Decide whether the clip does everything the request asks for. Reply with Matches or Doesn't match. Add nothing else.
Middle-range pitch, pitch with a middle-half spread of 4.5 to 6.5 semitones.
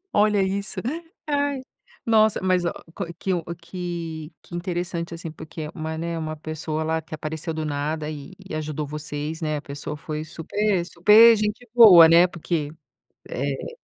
Doesn't match